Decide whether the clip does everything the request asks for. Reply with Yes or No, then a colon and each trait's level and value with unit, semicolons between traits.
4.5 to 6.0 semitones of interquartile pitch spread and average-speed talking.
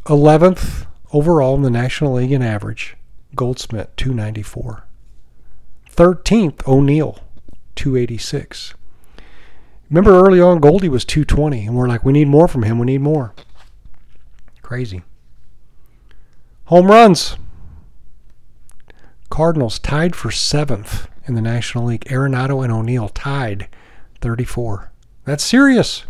No: average, 5.2 semitones; slow, 115 wpm